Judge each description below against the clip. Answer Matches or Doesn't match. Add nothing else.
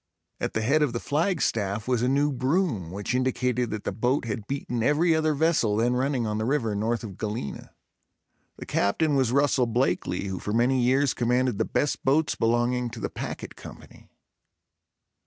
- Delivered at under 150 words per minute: Doesn't match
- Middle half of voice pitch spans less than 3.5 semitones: Doesn't match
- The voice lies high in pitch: Doesn't match